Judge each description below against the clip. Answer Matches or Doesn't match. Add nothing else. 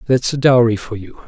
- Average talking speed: Doesn't match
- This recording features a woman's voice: Doesn't match